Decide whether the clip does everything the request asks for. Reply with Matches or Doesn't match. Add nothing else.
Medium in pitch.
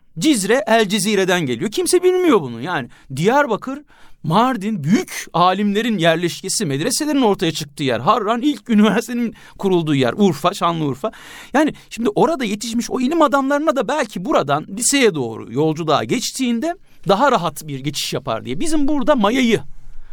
Doesn't match